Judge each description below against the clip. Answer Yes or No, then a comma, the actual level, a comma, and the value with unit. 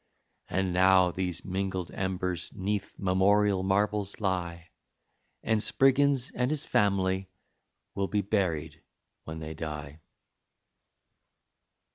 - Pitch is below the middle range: Yes, very low, 95 Hz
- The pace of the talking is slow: Yes, slow, 100 wpm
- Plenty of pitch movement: No, narrow, 2.4 semitones